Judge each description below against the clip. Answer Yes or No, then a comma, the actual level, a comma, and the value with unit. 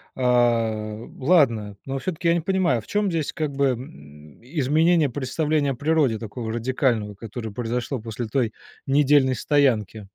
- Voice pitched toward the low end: Yes, low, 130 Hz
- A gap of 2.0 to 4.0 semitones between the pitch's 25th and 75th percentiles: No, average, 4.8 semitones